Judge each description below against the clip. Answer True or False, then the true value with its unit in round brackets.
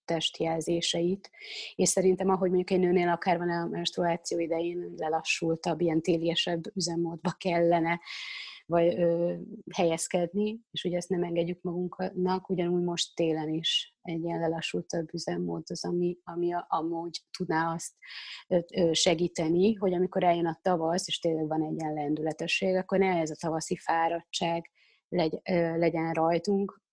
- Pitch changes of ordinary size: False (1.6 semitones)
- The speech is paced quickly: False (135 wpm)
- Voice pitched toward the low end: False (170 Hz)